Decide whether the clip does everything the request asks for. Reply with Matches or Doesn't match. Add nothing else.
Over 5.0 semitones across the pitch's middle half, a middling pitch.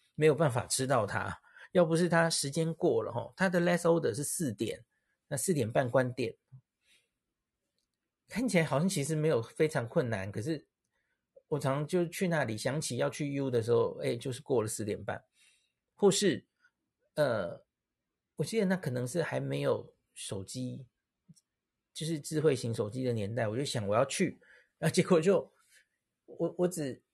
Matches